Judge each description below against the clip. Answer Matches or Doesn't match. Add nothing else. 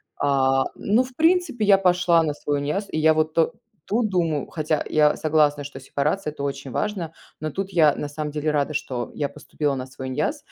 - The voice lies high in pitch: Doesn't match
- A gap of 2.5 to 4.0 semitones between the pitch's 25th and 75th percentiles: Doesn't match